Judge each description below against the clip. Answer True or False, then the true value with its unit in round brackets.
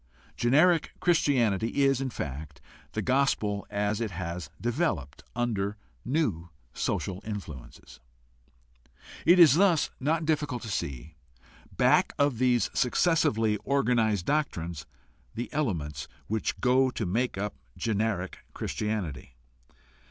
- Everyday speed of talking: False (110 wpm)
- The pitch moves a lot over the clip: True (6.8 semitones)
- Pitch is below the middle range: True (110 Hz)